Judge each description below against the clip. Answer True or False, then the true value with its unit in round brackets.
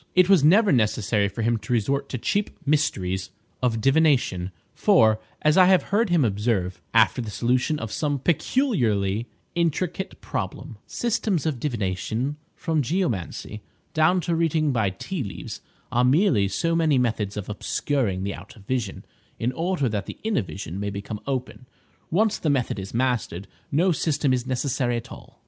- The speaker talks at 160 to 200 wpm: True (165 wpm)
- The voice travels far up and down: True (7.2 semitones)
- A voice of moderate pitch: False (125 Hz)